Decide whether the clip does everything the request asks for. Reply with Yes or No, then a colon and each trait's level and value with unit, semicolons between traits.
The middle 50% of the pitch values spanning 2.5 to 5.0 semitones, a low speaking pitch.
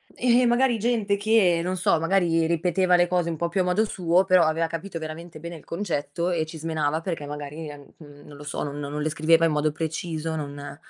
No: average, 2.8 semitones; medium, 165 Hz